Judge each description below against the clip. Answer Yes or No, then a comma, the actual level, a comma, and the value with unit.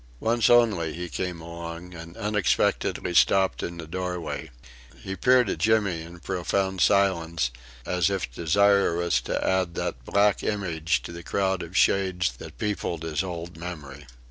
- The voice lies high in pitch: No, very low, 90 Hz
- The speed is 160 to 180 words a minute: No, average, 150 wpm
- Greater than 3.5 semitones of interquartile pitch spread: No, average, 2.8 semitones